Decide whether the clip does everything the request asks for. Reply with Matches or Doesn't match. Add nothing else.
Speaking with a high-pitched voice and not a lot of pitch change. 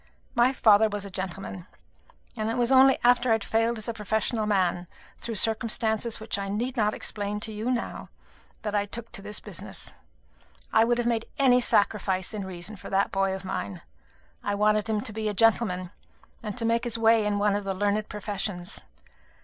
Matches